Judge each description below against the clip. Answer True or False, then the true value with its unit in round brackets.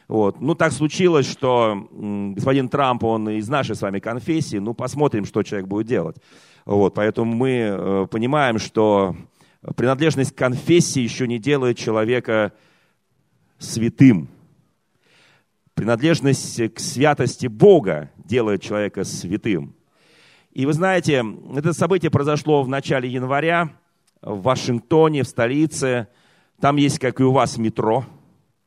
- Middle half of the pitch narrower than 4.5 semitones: False (5.1 semitones)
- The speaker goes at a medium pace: True (125 wpm)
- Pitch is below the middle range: True (130 Hz)